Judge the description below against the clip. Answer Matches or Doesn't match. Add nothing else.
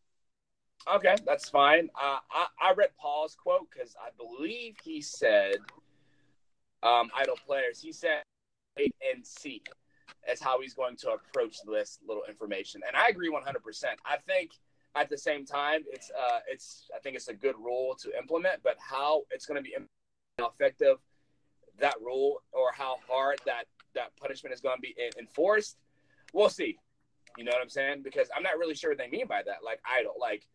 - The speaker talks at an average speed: Matches